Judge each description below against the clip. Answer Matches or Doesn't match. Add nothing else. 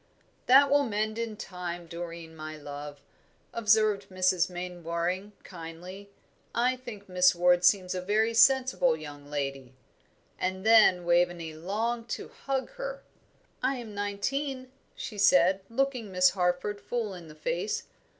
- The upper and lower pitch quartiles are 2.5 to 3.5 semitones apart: Doesn't match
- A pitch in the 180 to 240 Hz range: Matches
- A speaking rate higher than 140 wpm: Doesn't match